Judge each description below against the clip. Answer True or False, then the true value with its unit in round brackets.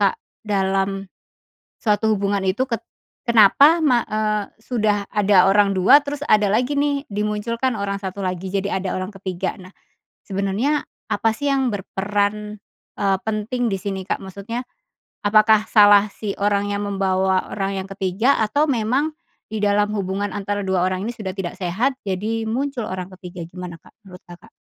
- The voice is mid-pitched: False (205 Hz)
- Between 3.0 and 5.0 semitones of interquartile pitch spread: False (2.4 semitones)